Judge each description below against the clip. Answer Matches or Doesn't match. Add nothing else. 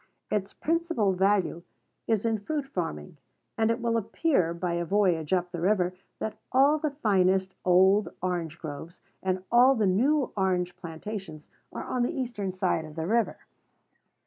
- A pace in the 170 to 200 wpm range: Doesn't match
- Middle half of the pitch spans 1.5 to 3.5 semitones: Doesn't match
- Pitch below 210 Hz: Matches